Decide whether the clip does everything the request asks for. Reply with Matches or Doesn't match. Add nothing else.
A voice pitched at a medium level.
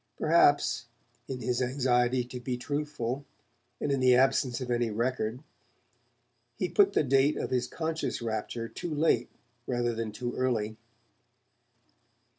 Doesn't match